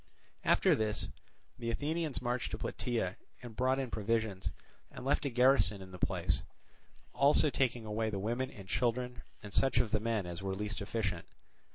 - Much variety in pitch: No, average, 3.6 semitones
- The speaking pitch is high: No, low, 115 Hz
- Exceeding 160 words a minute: Yes, average, 175 wpm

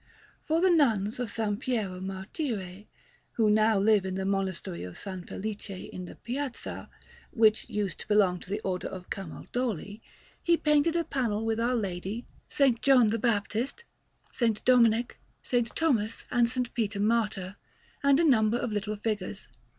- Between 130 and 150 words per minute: No, average, 160 wpm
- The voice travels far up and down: No, average, 3.9 semitones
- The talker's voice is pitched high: Yes, high, 215 Hz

